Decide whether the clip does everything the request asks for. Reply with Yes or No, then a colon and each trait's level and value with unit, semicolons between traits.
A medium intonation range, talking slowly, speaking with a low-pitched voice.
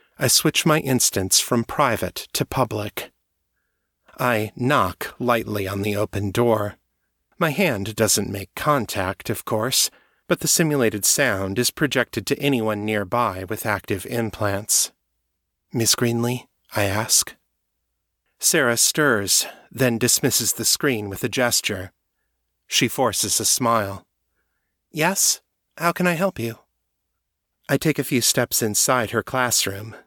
Yes: average, 4.2 semitones; slow, 130 wpm; low, 115 Hz